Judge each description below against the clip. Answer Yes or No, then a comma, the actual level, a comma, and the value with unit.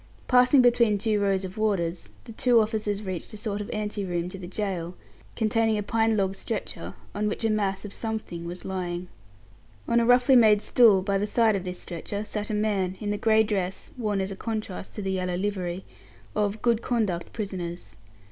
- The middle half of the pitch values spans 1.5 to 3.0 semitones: Yes, narrow, 2.6 semitones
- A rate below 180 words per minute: No, average, 200 wpm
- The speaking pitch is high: Yes, high, 205 Hz